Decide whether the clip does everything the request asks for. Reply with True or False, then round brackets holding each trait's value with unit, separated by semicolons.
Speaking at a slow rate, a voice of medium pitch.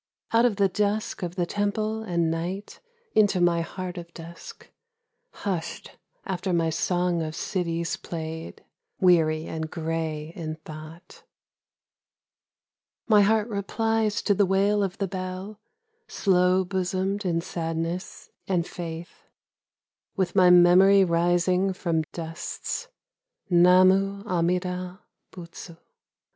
True (115 wpm; 180 Hz)